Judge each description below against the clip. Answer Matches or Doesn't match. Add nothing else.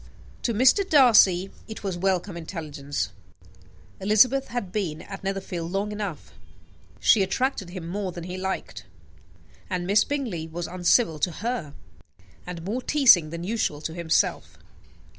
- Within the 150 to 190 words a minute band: Doesn't match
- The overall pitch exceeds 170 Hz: Matches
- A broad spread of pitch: Doesn't match